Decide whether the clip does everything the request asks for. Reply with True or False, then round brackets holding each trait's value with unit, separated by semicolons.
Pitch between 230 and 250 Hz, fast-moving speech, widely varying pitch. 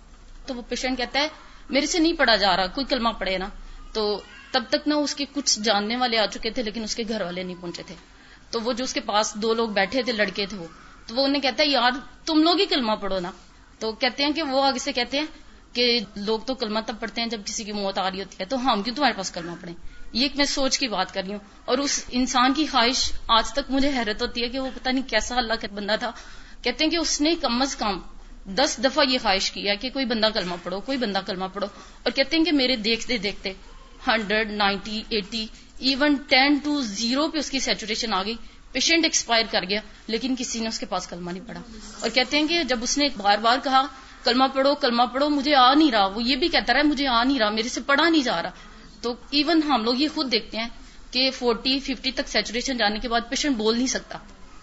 False (245 Hz; 235 wpm; 4.0 semitones)